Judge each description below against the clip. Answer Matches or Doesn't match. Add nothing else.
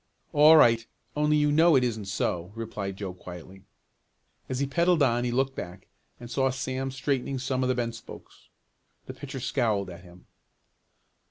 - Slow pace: Doesn't match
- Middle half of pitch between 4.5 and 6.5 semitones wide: Matches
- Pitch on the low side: Matches